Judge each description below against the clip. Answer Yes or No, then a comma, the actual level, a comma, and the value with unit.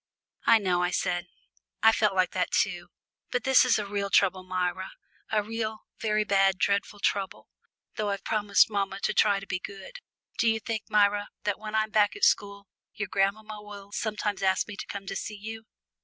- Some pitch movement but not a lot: No, narrow, 1.7 semitones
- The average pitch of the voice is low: No, high, 205 Hz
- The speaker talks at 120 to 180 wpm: No, average, 195 wpm